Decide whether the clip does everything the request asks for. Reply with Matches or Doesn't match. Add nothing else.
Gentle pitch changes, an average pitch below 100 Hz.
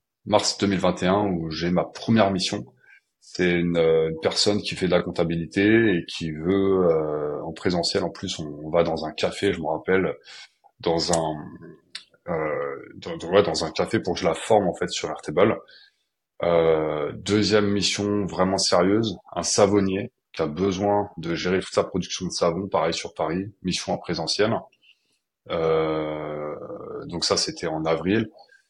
Doesn't match